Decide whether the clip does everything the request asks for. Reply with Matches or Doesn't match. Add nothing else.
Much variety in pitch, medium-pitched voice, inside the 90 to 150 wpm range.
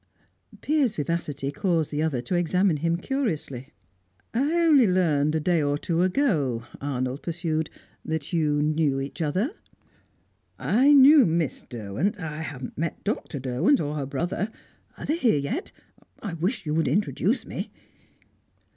Matches